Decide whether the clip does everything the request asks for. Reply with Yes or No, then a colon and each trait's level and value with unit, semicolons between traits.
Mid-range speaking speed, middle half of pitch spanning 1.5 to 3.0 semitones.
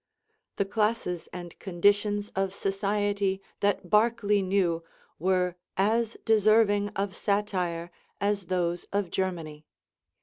No: slow, 105 wpm; narrow, 2.4 semitones